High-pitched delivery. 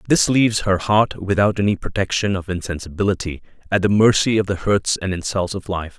No: low, 100 Hz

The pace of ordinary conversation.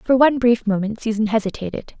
Yes: average, 180 wpm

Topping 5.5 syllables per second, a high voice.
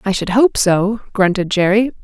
No: 4.7 syllables/s; high, 205 Hz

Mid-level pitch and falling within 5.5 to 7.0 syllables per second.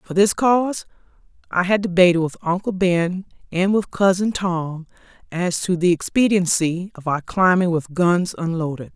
No: medium, 180 Hz; 4.6 syllables/s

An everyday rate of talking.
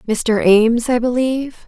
Yes: average, 145 wpm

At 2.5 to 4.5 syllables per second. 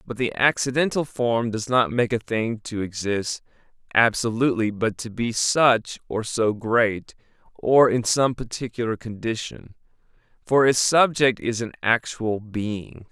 Yes: 4.1 syllables/s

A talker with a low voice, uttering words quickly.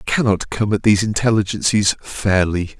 No: low, 105 Hz; average, 150 wpm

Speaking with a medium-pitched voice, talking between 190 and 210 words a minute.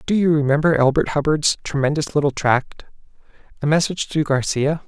No: medium, 150 Hz; average, 150 wpm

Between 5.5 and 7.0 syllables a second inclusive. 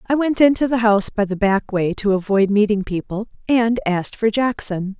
No: 5.2 syllables/s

